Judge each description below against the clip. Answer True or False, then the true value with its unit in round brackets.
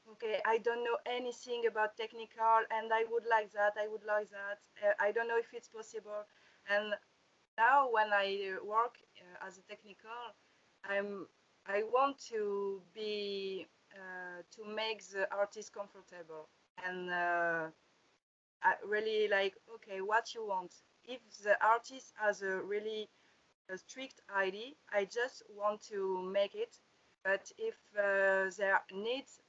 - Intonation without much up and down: True (2.3 semitones)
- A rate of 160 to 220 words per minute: False (145 wpm)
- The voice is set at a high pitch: True (210 Hz)